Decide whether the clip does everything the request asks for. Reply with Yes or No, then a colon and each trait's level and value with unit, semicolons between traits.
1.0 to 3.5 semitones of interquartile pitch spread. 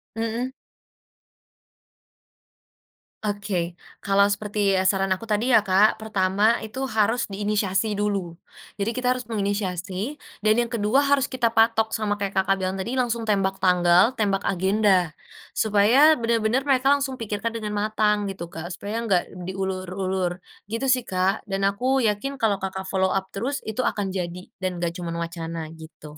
Yes: average, 3.2 semitones